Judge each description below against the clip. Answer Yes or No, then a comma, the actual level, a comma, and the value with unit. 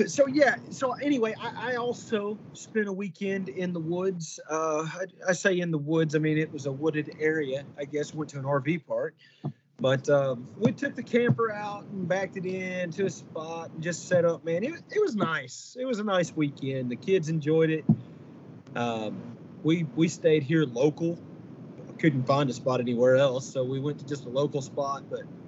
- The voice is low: No, medium, 160 Hz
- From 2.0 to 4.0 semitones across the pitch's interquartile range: No, average, 4.8 semitones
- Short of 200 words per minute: No, fast, 205 wpm